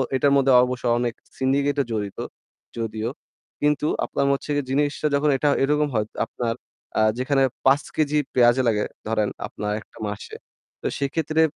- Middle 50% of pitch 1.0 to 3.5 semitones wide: No, average, 4.0 semitones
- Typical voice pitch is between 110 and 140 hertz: Yes, low, 135 Hz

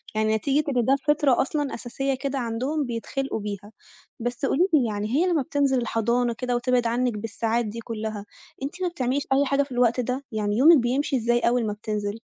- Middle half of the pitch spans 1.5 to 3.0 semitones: No, average, 3.4 semitones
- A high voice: Yes, high, 245 Hz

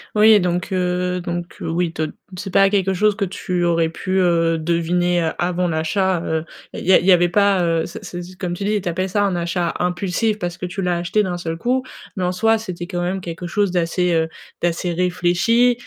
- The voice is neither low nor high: Yes, medium, 180 Hz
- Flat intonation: Yes, narrow, 1.8 semitones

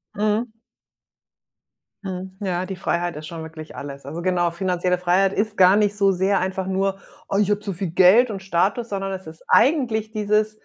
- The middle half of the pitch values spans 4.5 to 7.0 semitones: No, average, 2.7 semitones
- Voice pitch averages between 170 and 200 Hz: Yes, high, 190 Hz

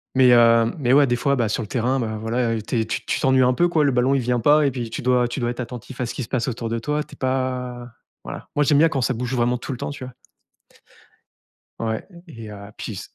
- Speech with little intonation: Yes, narrow, 2.2 semitones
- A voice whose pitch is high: No, low, 125 Hz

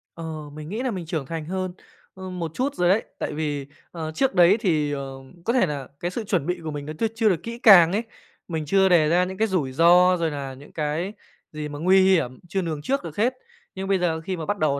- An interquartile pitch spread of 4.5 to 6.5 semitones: No, average, 3.8 semitones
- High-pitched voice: No, medium, 170 Hz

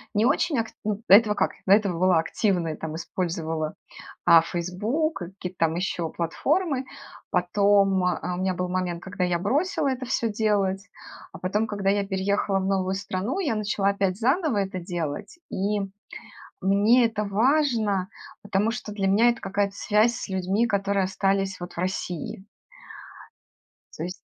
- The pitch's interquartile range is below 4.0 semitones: Yes, average, 2.8 semitones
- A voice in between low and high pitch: No, high, 195 Hz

